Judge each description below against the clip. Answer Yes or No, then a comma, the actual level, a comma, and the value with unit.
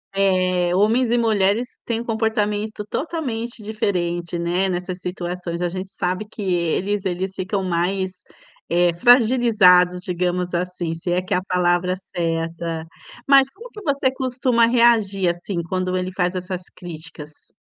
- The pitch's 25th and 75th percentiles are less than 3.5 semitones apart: No, average, 3.8 semitones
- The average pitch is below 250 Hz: Yes, medium, 185 Hz